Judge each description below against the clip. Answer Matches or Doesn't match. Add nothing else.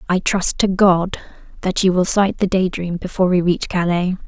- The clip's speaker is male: Doesn't match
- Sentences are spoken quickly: Matches